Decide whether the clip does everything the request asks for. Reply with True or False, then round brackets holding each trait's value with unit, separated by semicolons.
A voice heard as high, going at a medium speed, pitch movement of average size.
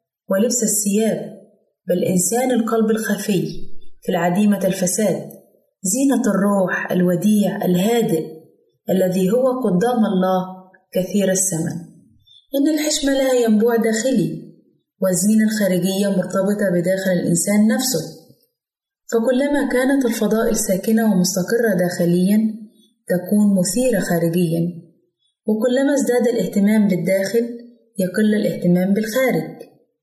True (205 Hz; 90 wpm; 4.1 semitones)